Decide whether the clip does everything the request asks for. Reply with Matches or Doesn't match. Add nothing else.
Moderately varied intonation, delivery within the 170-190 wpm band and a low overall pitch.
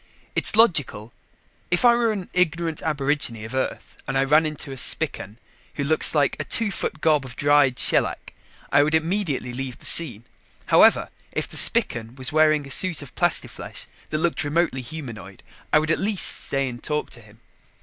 Doesn't match